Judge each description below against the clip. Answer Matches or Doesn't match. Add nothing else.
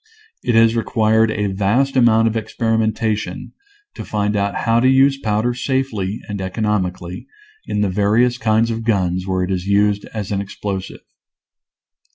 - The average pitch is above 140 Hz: Doesn't match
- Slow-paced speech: Doesn't match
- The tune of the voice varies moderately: Doesn't match